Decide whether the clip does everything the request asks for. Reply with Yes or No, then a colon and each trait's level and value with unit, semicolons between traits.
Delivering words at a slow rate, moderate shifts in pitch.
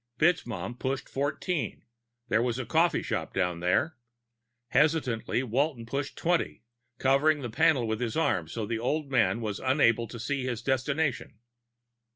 No: average, 155 wpm; average, 4.2 semitones